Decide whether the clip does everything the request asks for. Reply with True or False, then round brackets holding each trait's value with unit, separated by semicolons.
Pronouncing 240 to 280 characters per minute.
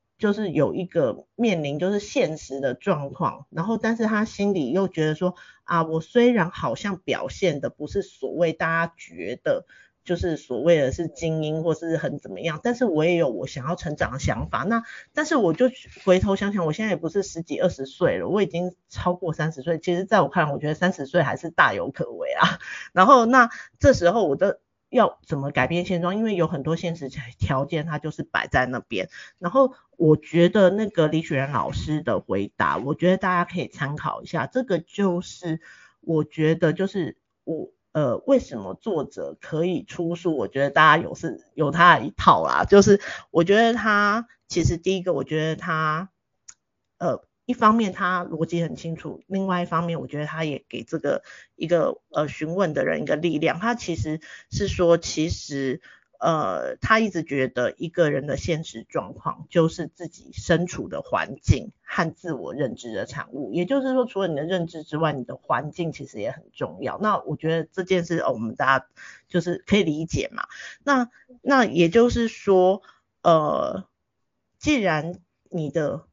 True (270 characters per minute)